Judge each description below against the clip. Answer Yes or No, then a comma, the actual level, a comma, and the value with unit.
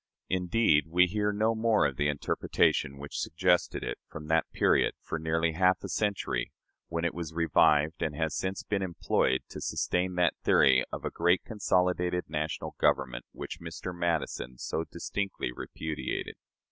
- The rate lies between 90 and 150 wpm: No, average, 160 wpm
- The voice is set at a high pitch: No, very low, 85 Hz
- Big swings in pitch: No, average, 3.0 semitones